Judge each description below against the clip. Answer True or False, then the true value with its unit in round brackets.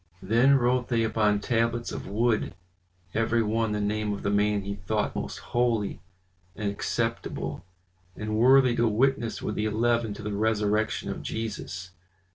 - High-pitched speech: False (110 Hz)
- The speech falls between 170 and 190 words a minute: False (155 wpm)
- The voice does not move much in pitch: True (2.1 semitones)